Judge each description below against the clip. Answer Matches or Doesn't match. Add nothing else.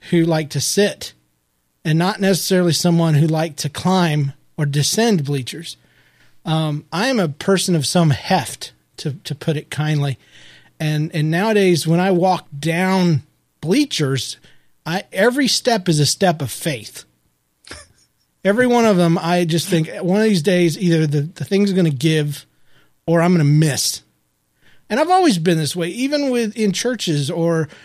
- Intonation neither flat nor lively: Matches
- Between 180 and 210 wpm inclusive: Doesn't match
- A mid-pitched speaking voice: Matches